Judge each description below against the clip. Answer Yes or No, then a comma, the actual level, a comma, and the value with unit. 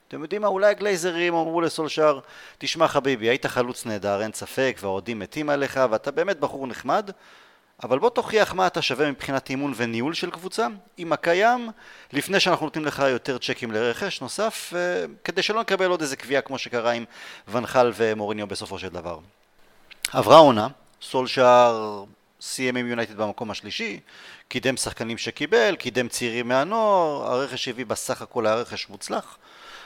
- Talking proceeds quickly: Yes, fast, 155 wpm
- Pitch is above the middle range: No, low, 135 Hz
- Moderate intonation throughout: No, wide, 6.5 semitones